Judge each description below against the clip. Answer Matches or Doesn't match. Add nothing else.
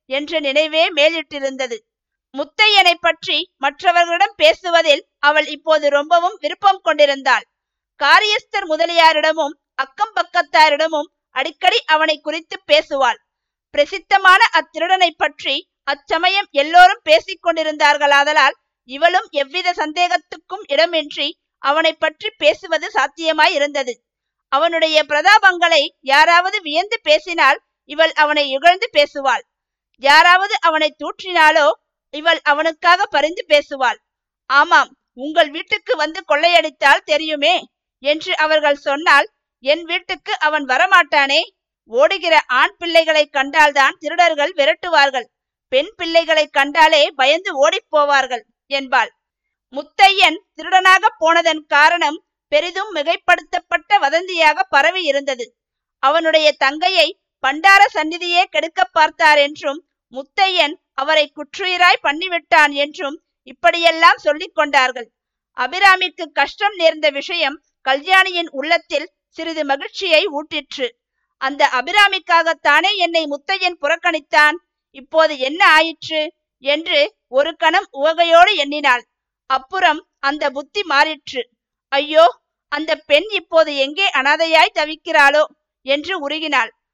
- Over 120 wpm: Doesn't match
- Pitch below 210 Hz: Doesn't match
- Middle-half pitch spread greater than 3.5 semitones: Doesn't match